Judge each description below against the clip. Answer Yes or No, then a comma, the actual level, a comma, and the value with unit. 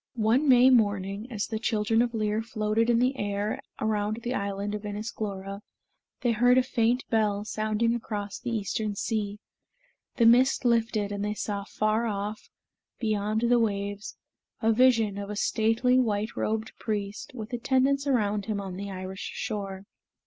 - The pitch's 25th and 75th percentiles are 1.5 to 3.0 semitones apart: Yes, narrow, 2.4 semitones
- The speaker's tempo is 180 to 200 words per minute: No, average, 165 wpm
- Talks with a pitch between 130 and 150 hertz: No, high, 215 Hz